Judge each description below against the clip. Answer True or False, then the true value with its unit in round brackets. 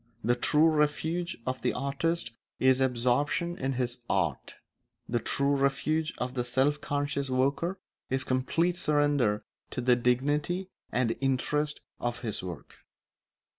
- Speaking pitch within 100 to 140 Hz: True (135 Hz)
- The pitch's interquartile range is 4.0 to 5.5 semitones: False (3.1 semitones)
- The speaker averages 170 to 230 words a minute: False (135 wpm)